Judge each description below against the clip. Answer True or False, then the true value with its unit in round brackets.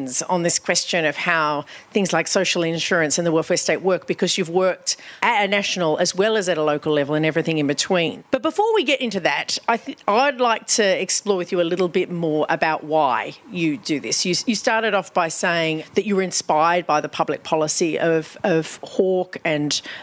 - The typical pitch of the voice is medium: True (180 Hz)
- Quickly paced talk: True (215 wpm)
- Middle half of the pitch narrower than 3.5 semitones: False (3.9 semitones)